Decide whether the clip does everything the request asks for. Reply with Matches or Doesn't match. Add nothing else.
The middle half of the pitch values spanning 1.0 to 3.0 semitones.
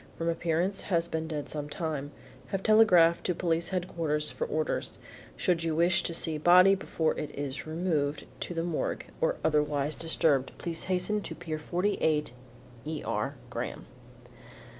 Matches